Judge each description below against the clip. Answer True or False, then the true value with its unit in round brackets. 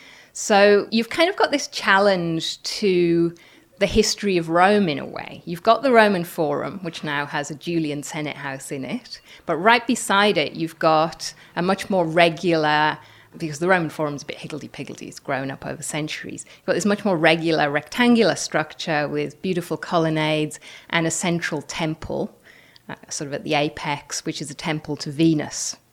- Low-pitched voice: False (165 Hz)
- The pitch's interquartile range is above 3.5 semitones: True (4.2 semitones)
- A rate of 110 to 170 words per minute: False (185 wpm)